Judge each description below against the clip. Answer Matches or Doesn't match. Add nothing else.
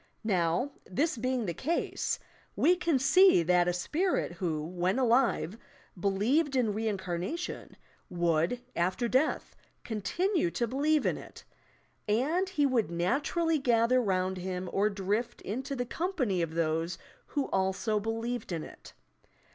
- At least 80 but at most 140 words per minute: Matches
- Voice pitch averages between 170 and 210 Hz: Doesn't match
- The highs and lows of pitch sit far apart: Matches